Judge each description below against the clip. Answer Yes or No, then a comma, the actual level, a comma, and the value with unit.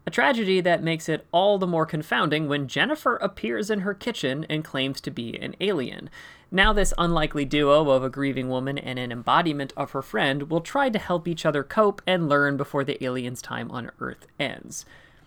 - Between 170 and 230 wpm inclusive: Yes, average, 200 wpm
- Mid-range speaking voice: Yes, medium, 155 Hz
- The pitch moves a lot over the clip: No, average, 4.9 semitones